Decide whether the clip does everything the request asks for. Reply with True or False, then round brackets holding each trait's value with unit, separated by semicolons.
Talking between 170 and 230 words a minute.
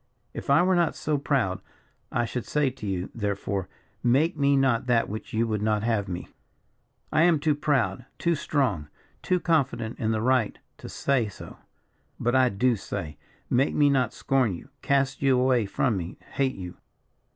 True (180 wpm)